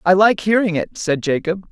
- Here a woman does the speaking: Yes, female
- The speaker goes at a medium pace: No, fast, 210 wpm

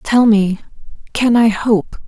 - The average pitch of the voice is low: No, high, 220 Hz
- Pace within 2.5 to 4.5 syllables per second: Yes, 3.5 syllables/s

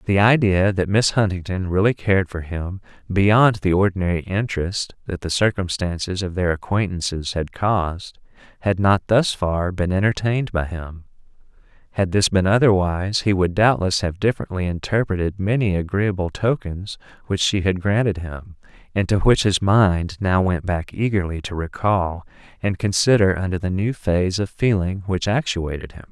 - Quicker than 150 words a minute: Yes, average, 160 wpm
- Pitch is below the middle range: Yes, very low, 95 Hz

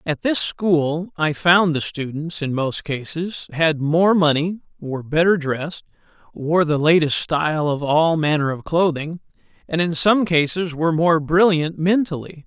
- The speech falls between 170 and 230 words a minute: No, average, 160 wpm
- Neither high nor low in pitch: Yes, medium, 160 Hz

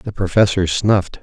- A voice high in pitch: No, low, 100 Hz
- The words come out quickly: No, average, 145 wpm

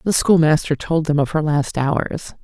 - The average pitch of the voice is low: No, medium, 155 Hz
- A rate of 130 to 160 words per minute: No, average, 200 wpm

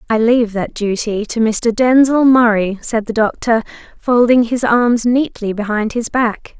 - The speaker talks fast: No, average, 165 wpm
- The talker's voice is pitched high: Yes, high, 230 Hz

